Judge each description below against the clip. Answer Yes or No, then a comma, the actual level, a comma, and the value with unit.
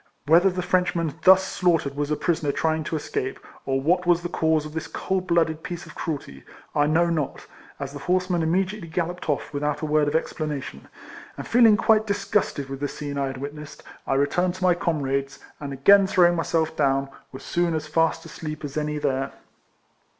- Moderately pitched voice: Yes, medium, 160 Hz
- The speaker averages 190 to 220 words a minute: Yes, average, 200 wpm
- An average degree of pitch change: Yes, average, 3.5 semitones